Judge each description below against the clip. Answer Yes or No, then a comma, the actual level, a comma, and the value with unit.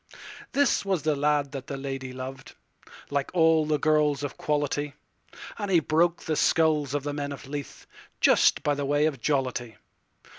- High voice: No, medium, 145 Hz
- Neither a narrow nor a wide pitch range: No, narrow, 1.9 semitones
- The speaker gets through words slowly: No, average, 150 wpm